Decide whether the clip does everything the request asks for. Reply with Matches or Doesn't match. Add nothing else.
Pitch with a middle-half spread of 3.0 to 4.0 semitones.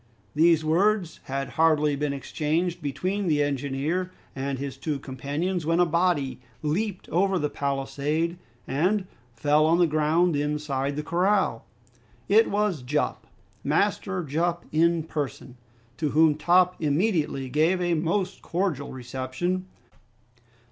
Matches